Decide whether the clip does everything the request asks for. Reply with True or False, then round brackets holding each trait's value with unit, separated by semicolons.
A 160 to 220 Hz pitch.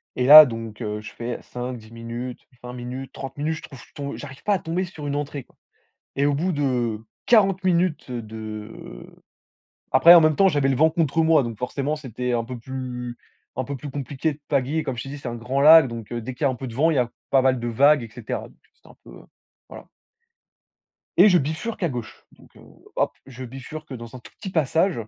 False (135 Hz)